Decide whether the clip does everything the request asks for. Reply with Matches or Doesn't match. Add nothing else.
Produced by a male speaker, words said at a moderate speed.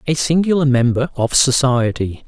Doesn't match